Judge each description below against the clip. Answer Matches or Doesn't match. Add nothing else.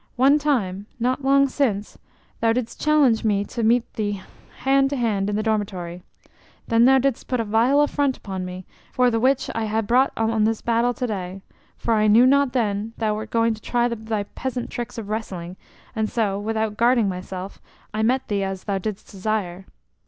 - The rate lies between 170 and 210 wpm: Matches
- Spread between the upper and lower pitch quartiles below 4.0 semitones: Matches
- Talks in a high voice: Matches